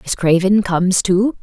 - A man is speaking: No, female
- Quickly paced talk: No, average, 170 wpm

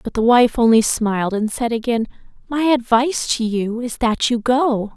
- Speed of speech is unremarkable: Yes, average, 195 wpm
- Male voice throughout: No, female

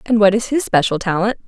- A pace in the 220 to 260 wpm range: Yes, fast, 245 wpm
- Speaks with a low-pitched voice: No, high, 210 Hz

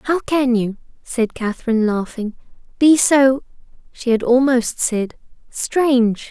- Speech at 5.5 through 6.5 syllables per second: No, 4.0 syllables/s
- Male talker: No, female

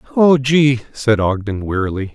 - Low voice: Yes, low, 120 Hz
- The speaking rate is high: No, average, 140 wpm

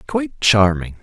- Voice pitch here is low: Yes, low, 100 Hz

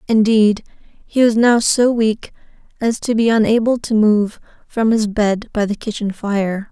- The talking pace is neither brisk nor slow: Yes, average, 170 wpm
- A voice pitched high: Yes, high, 220 Hz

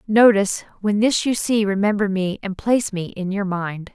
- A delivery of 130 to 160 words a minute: No, average, 200 wpm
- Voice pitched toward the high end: Yes, high, 200 Hz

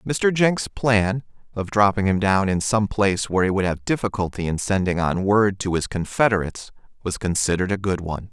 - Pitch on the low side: Yes, low, 100 Hz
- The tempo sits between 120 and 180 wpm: No, average, 195 wpm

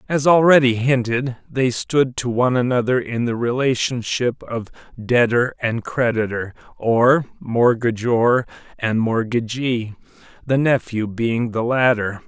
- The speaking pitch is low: Yes, low, 120 Hz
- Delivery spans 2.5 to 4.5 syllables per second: Yes, 4.0 syllables/s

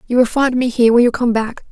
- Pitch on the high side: Yes, high, 240 Hz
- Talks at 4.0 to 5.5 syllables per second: No, 6.7 syllables/s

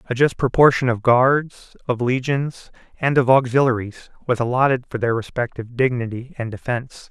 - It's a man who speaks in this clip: Yes, male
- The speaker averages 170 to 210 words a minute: No, average, 150 wpm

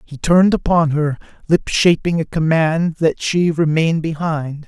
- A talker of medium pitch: Yes, medium, 160 Hz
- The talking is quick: No, average, 155 wpm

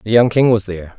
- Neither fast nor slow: No, fast, 305 wpm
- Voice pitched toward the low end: Yes, low, 110 Hz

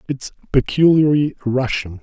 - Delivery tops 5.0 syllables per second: No, 4.5 syllables/s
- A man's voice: Yes, male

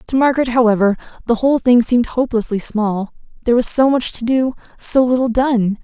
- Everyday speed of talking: Yes, average, 185 wpm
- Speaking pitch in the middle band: No, high, 240 Hz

